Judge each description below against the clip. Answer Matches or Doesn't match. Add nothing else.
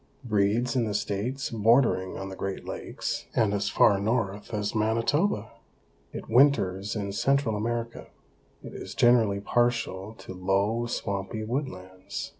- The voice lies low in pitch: Matches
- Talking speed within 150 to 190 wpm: Doesn't match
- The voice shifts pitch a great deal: Doesn't match